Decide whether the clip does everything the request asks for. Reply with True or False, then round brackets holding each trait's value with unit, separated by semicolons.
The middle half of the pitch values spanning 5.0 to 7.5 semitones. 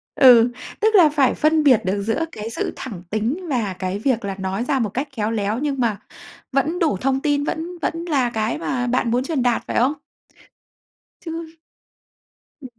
True (5.4 semitones)